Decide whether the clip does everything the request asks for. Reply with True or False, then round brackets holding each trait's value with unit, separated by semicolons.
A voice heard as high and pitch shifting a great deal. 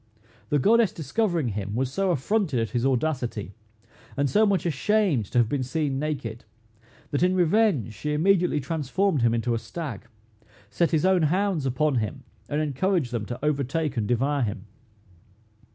False (145 Hz; 6.3 semitones)